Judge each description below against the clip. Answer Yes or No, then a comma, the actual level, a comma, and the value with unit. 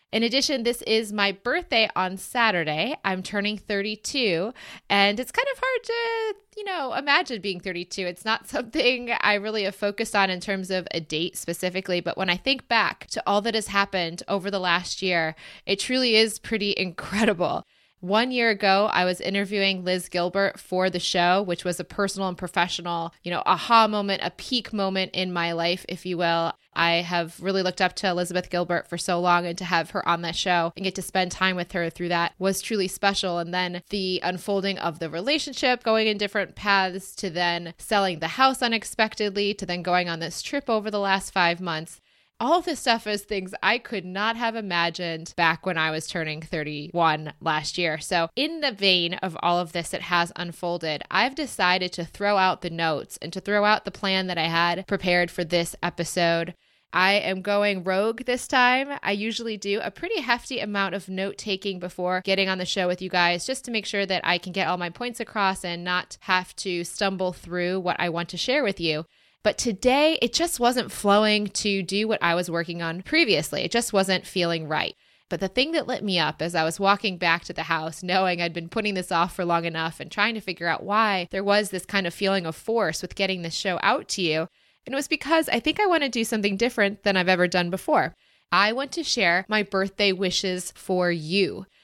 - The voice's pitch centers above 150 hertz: Yes, high, 190 Hz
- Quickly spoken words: Yes, fast, 215 wpm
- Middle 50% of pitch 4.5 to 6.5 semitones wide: No, average, 3.5 semitones